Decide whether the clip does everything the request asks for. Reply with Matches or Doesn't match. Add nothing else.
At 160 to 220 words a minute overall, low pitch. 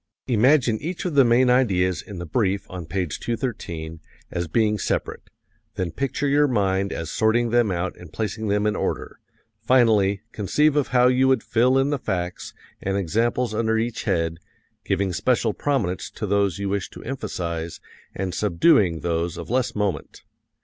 Matches